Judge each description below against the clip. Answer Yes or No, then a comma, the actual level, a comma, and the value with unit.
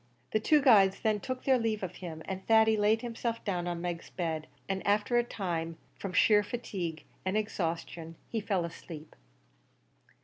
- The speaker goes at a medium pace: Yes, average, 170 wpm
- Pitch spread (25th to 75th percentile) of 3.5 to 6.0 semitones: Yes, average, 4.4 semitones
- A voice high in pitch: Yes, high, 195 Hz